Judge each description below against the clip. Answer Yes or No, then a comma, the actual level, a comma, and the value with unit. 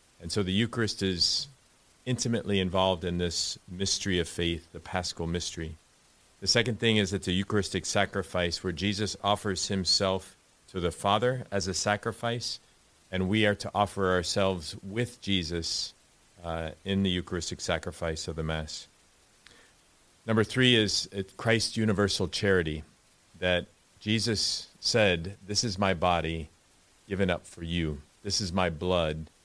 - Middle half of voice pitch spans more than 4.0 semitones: No, average, 3.0 semitones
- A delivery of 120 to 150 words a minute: Yes, average, 145 wpm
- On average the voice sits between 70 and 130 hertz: Yes, very low, 95 Hz